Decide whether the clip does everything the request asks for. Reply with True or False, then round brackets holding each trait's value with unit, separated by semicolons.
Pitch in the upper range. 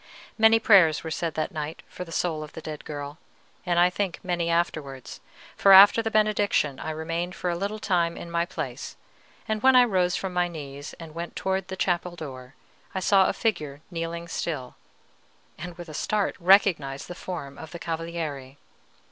False (170 Hz)